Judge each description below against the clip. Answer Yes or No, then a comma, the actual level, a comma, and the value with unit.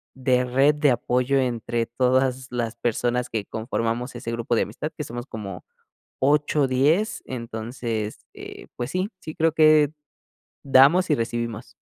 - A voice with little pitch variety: No, average, 3.4 semitones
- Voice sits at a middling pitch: No, low, 125 Hz